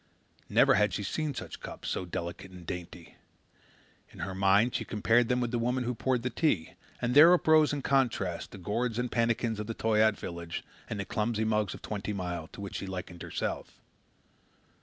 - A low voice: Yes, low, 110 Hz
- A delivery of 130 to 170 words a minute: No, average, 195 wpm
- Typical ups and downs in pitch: Yes, average, 4.6 semitones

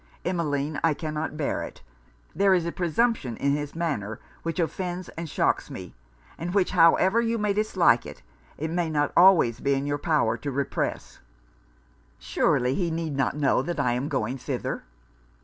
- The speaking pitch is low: No, medium, 160 Hz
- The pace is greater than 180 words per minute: No, average, 170 wpm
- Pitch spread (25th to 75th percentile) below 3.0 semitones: No, average, 4.0 semitones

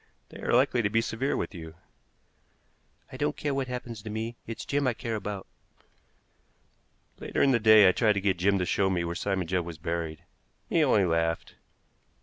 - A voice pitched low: Yes, low, 105 Hz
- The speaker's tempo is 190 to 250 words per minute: Yes, average, 195 wpm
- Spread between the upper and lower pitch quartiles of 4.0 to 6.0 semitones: Yes, average, 5.0 semitones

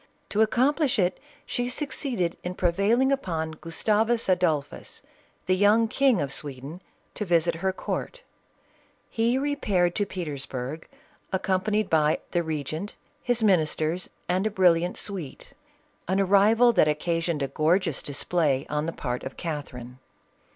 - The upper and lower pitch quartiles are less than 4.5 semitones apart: No, wide, 5.4 semitones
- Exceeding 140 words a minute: No, slow, 135 wpm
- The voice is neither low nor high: Yes, medium, 180 Hz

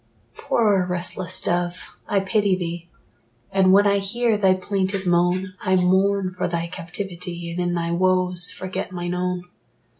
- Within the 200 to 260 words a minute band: No, average, 150 wpm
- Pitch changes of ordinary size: No, narrow, 1.7 semitones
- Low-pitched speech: No, medium, 185 Hz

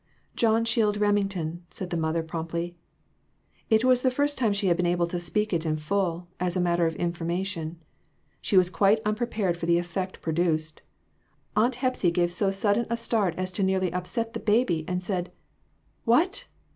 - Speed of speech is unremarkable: Yes, average, 180 wpm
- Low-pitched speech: No, medium, 185 Hz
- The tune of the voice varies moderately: Yes, average, 3.7 semitones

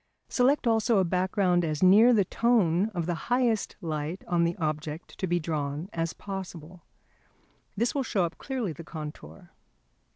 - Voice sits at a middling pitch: Yes, medium, 180 Hz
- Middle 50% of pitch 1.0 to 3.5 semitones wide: No, average, 5.1 semitones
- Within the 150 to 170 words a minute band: Yes, average, 160 wpm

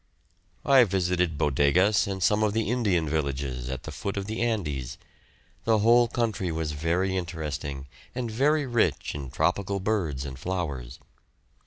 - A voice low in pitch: Yes, very low, 90 Hz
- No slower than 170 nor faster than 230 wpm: No, average, 150 wpm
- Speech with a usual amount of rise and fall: No, wide, 6.8 semitones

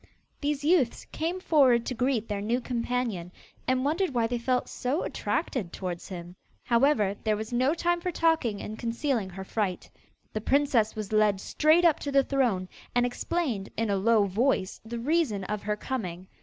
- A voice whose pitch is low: No, high, 235 Hz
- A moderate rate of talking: Yes, average, 180 wpm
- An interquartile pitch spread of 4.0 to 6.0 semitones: Yes, average, 5.1 semitones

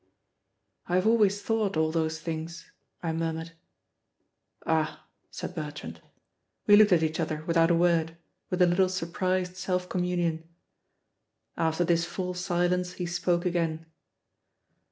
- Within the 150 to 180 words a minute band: No, slow, 135 wpm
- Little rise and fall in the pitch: Yes, narrow, 2.0 semitones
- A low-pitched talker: No, medium, 175 Hz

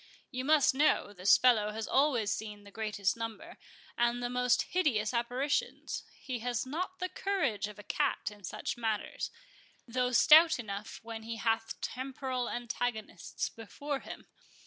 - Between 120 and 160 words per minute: Yes, average, 150 wpm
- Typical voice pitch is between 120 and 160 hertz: No, high, 240 Hz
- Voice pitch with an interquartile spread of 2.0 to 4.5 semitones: Yes, average, 3.4 semitones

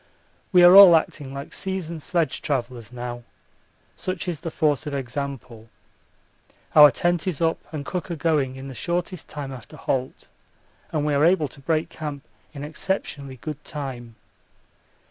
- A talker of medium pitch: Yes, medium, 150 Hz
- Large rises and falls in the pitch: No, average, 3.9 semitones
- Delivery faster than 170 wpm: No, average, 155 wpm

